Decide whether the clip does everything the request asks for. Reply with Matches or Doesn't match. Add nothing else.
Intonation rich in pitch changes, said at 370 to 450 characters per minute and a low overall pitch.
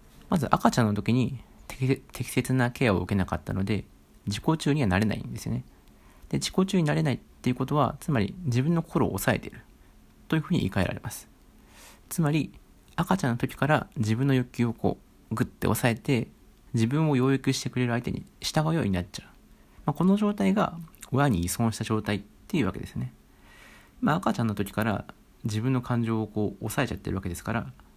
Matches